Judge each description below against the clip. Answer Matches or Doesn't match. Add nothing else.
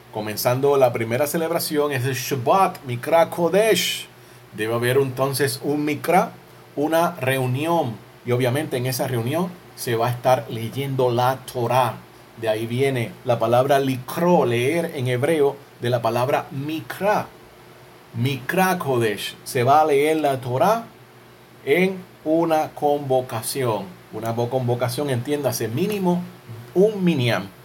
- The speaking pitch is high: Doesn't match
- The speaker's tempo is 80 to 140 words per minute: Matches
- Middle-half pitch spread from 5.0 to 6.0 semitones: Doesn't match